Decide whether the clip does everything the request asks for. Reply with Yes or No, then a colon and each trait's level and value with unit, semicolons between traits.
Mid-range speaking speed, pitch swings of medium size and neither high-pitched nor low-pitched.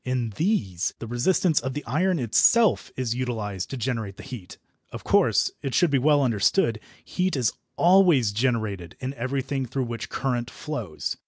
No: average, 165 wpm; average, 4.4 semitones; low, 125 Hz